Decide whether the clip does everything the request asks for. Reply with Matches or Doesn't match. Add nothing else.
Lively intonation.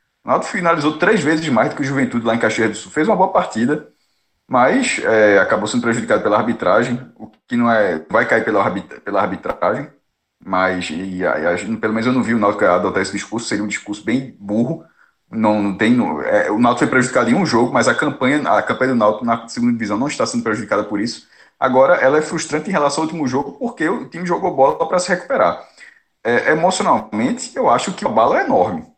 Matches